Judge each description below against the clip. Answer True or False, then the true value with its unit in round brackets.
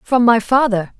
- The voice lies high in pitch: True (225 Hz)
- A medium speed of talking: True (180 wpm)